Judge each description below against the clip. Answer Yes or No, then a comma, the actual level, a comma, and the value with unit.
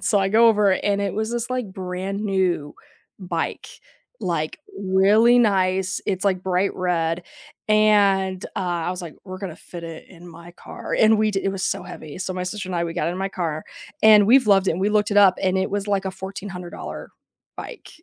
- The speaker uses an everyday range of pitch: No, narrow, 2.2 semitones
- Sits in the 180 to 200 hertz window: Yes, high, 190 Hz